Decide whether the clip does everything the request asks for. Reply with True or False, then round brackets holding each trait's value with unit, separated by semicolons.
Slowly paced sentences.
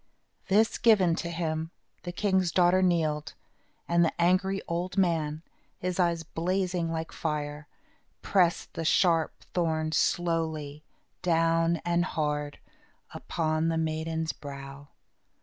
True (115 wpm)